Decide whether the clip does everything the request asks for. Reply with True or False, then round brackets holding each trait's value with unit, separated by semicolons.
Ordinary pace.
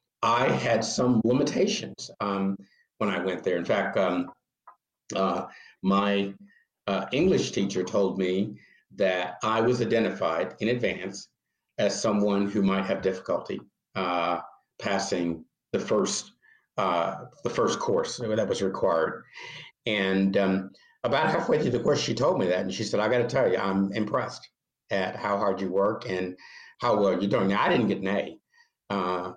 True (165 wpm)